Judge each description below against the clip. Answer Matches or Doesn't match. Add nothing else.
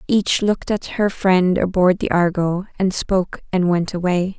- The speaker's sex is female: Matches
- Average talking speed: Matches